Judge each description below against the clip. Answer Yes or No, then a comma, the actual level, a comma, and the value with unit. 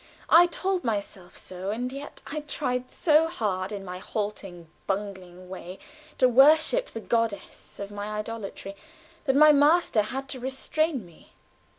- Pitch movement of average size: No, wide, 6.6 semitones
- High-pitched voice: Yes, high, 230 Hz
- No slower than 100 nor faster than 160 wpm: Yes, average, 150 wpm